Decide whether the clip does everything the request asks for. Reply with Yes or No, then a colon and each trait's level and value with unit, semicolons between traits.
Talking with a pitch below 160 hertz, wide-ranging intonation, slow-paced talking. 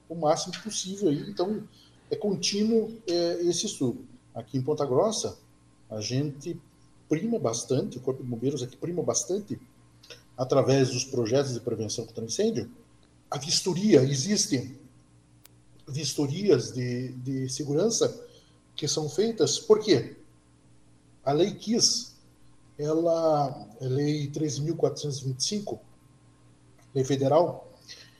Yes: low, 135 Hz; wide, 7.2 semitones; slow, 110 wpm